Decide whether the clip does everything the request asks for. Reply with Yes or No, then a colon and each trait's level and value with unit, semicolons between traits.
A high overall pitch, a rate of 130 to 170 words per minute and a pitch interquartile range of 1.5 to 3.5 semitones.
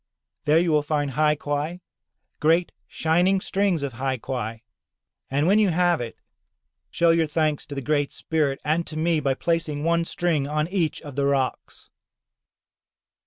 No: medium, 155 Hz; average, 165 wpm; average, 3.0 semitones